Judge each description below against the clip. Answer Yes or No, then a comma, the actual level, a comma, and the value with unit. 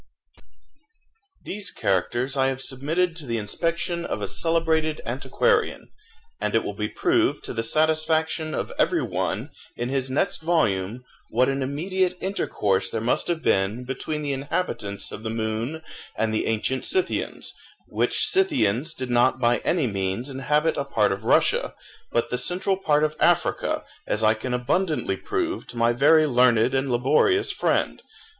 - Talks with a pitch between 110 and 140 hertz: Yes, low, 135 Hz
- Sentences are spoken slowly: No, average, 160 wpm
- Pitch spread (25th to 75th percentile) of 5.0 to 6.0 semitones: Yes, wide, 5.6 semitones